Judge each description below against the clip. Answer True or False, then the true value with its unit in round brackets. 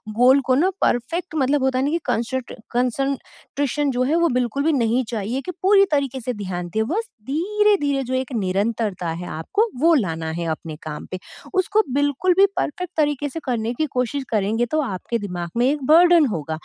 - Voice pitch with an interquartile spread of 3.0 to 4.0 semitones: False (5.2 semitones)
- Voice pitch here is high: True (260 Hz)